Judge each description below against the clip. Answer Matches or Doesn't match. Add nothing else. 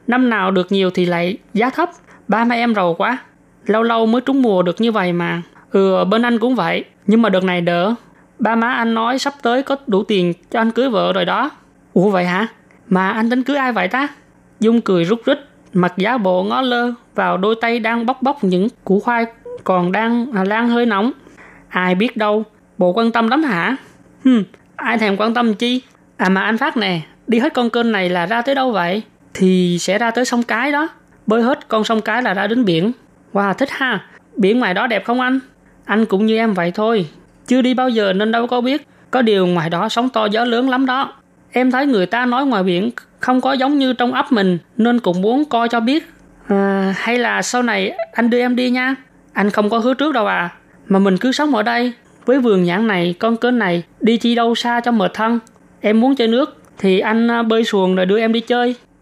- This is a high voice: Matches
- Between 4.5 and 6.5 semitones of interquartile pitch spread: Doesn't match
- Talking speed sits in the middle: Matches